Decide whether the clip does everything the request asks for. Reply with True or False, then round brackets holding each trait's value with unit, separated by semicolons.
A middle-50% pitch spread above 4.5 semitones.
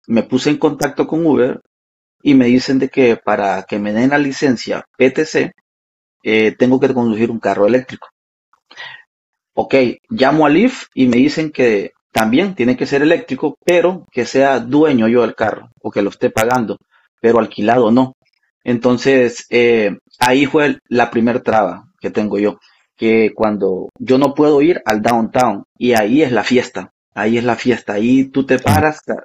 False (3.8 semitones)